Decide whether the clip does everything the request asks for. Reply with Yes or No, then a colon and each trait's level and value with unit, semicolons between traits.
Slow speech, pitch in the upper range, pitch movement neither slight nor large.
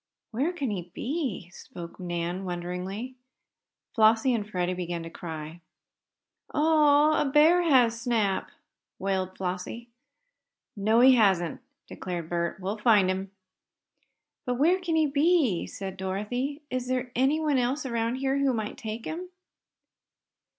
No: slow, 130 wpm; high, 225 Hz; wide, 6.6 semitones